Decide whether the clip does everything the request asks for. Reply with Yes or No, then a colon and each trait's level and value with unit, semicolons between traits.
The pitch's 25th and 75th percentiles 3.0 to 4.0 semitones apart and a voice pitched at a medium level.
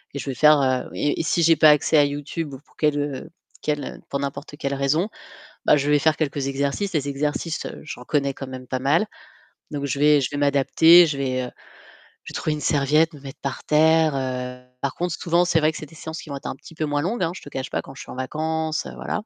No: narrow, 2.4 semitones; medium, 145 Hz